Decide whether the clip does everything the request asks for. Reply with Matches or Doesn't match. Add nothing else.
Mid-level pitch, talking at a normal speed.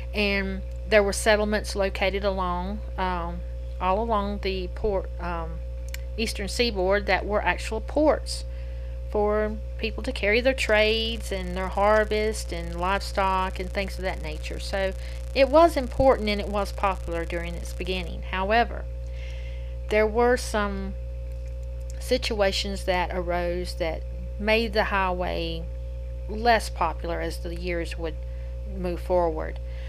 Doesn't match